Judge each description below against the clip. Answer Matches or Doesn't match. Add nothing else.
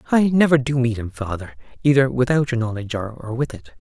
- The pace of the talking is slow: Doesn't match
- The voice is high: Doesn't match